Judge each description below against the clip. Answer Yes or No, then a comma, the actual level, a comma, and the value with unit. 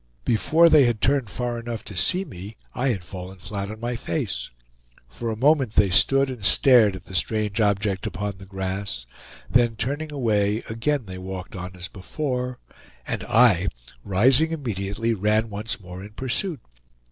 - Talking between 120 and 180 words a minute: Yes, average, 170 wpm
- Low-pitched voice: Yes, low, 110 Hz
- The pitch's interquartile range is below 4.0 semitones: No, average, 4.6 semitones